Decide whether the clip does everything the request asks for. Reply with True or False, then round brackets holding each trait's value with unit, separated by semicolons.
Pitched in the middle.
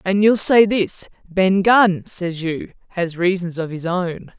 True (180 Hz)